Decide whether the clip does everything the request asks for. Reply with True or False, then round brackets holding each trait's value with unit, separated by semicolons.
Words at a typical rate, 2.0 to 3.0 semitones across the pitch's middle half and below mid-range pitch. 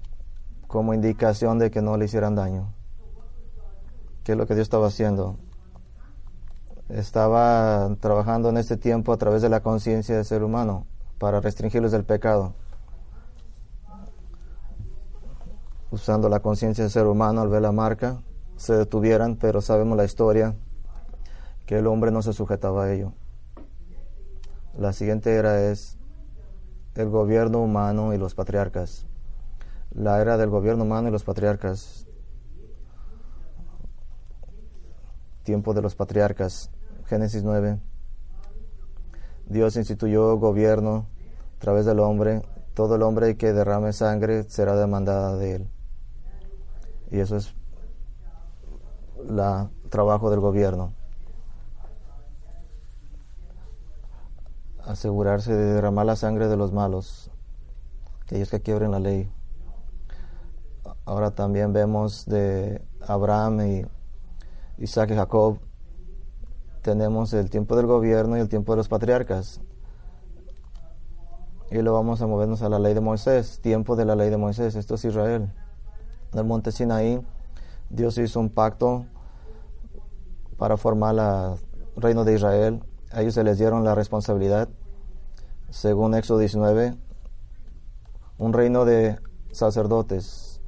False (120 wpm; 2.5 semitones; 105 Hz)